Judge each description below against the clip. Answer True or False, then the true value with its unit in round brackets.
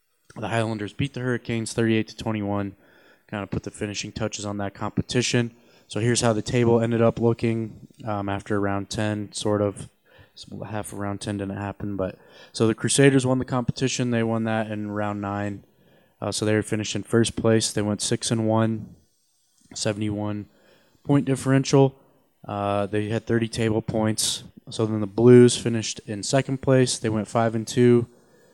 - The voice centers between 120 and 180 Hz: False (110 Hz)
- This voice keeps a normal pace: True (180 wpm)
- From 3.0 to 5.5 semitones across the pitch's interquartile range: False (2.5 semitones)